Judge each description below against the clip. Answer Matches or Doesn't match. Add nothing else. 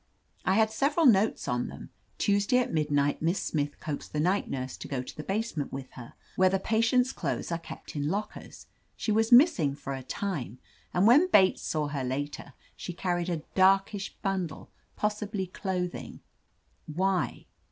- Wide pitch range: Matches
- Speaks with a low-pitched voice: Doesn't match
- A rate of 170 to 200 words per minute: Matches